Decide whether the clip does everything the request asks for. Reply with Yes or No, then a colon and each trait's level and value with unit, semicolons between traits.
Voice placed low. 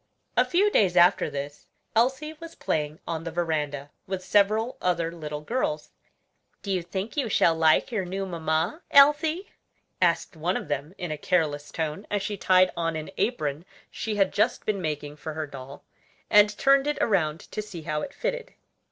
No: medium, 175 Hz